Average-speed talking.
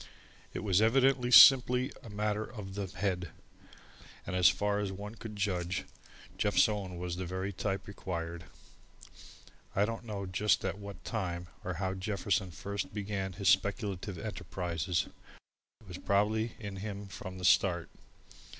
Yes: average, 150 wpm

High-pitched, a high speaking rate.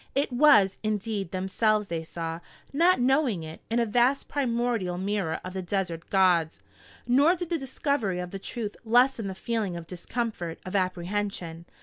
No: high, 205 Hz; average, 160 wpm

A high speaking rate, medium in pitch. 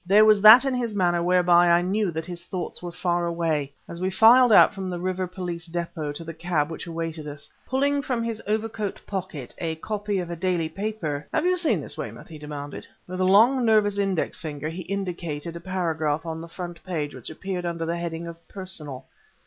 Yes: fast, 215 wpm; medium, 175 Hz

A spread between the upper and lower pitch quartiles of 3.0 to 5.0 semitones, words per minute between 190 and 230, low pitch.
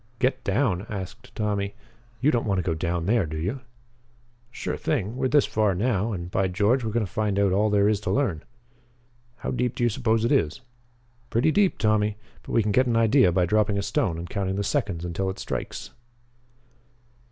Yes: average, 3.8 semitones; fast, 205 wpm; low, 105 Hz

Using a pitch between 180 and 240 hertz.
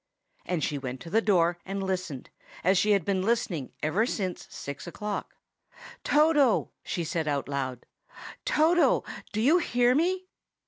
Yes: high, 190 Hz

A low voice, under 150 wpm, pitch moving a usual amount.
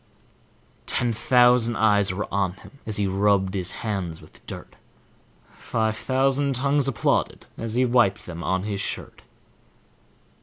Yes: low, 110 Hz; average, 140 wpm; average, 4.1 semitones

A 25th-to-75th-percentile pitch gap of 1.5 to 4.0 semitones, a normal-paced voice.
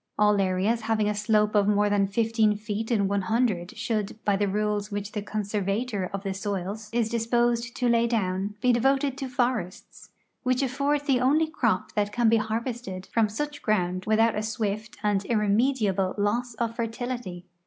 Yes: average, 2.7 semitones; average, 180 wpm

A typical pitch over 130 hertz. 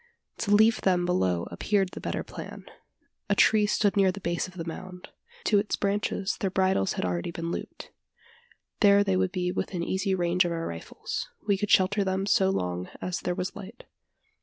Yes: medium, 185 Hz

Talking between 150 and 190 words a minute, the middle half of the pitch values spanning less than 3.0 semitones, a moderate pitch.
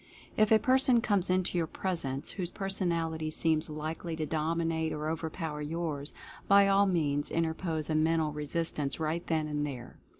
Yes: average, 170 wpm; narrow, 2.5 semitones; medium, 160 Hz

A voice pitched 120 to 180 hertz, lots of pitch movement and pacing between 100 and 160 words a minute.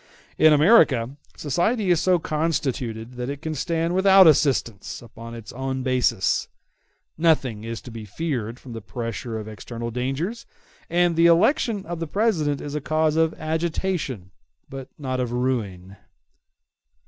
Yes: medium, 140 Hz; wide, 5.9 semitones; average, 150 wpm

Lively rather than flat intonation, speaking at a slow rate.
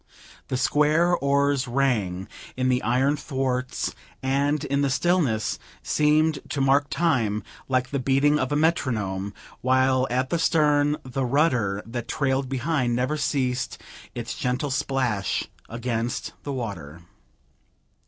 No: average, 2.9 semitones; slow, 130 wpm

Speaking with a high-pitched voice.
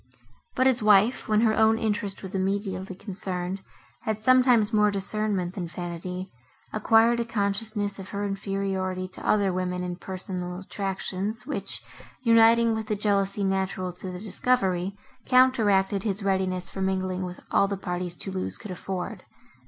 Yes: high, 195 Hz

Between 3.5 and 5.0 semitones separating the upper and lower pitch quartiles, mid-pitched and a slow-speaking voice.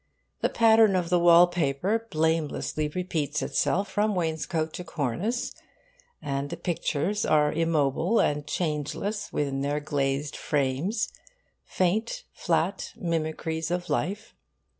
Yes: average, 3.8 semitones; medium, 165 Hz; slow, 115 wpm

